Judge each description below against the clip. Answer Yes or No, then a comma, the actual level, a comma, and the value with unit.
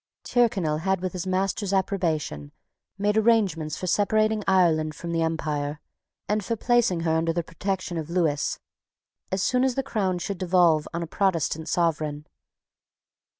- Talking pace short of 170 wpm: Yes, average, 150 wpm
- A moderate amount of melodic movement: Yes, average, 3.8 semitones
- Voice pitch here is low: No, medium, 180 Hz